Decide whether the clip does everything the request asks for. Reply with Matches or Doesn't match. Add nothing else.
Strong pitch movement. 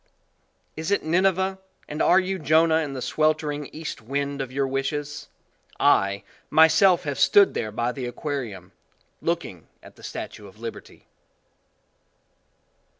Doesn't match